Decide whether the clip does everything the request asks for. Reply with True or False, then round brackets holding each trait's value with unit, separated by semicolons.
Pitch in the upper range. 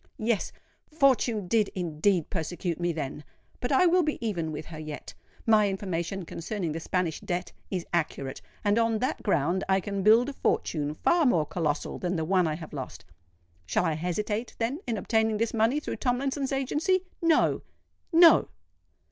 True (195 Hz)